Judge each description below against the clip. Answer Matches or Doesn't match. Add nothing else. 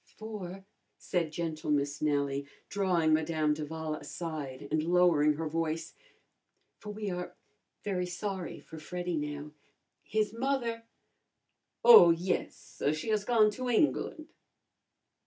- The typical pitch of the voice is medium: Matches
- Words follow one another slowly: Matches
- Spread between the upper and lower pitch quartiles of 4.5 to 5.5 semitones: Matches